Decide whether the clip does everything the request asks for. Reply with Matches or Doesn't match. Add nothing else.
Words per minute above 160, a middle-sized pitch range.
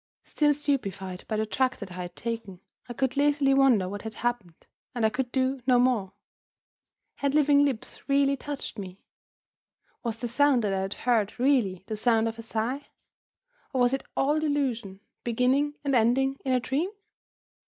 Matches